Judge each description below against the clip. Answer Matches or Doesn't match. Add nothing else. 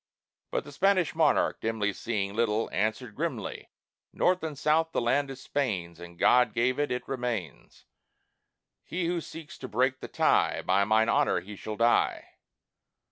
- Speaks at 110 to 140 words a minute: Doesn't match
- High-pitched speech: Doesn't match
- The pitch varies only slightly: Doesn't match